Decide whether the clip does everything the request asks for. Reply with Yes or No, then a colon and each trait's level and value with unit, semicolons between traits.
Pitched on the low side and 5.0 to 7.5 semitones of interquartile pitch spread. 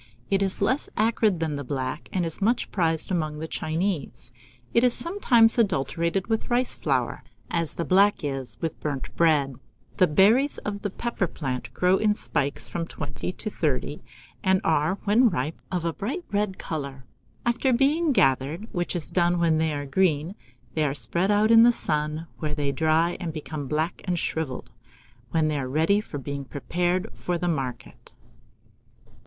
No: medium, 170 Hz; wide, 5.4 semitones